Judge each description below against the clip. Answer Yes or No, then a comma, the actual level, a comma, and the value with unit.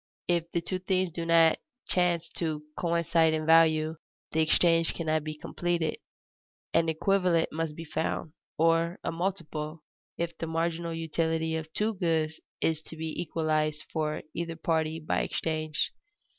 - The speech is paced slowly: No, average, 145 wpm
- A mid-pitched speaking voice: Yes, medium, 165 Hz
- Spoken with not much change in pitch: Yes, narrow, 1.2 semitones